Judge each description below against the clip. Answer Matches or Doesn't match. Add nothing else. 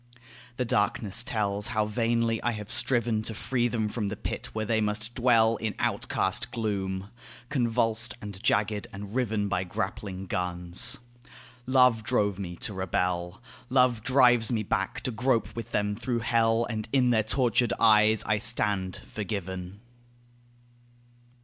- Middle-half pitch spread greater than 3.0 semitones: Doesn't match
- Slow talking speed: Doesn't match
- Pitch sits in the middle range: Doesn't match